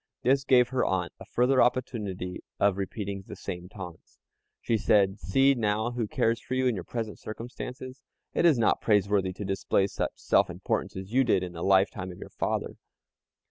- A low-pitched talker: Yes, low, 105 Hz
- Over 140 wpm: Yes, average, 185 wpm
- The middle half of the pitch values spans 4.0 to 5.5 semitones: Yes, average, 4.5 semitones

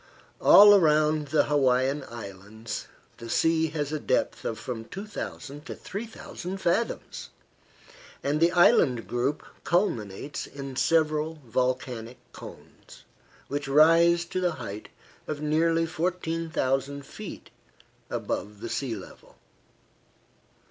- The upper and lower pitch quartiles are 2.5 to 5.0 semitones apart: Yes, average, 4.7 semitones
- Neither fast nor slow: No, slow, 110 wpm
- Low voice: No, medium, 150 Hz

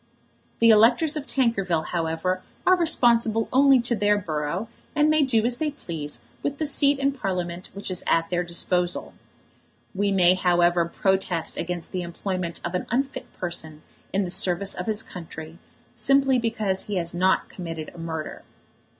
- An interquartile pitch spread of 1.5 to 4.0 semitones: No, wide, 5.5 semitones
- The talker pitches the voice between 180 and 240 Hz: Yes, high, 190 Hz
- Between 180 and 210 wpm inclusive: No, average, 165 wpm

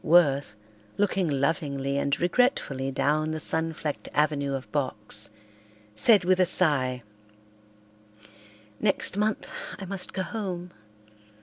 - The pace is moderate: No, slow, 115 wpm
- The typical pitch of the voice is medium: Yes, medium, 155 Hz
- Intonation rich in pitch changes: No, average, 4.8 semitones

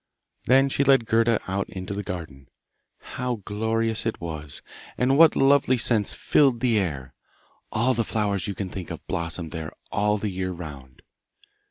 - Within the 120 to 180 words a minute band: Yes, average, 165 wpm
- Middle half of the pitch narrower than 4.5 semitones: No, average, 5.2 semitones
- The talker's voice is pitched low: Yes, low, 105 Hz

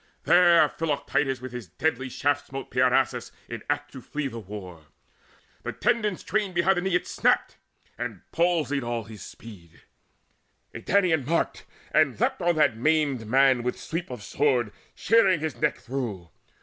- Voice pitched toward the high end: No, medium, 140 Hz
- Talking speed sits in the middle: Yes, average, 160 wpm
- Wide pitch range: Yes, wide, 5.7 semitones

